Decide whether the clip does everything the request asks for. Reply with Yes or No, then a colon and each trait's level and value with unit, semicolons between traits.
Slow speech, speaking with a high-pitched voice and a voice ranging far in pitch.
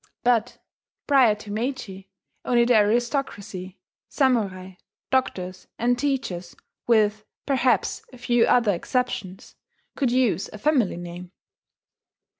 No: slow, 105 wpm; high, 225 Hz; average, 4.8 semitones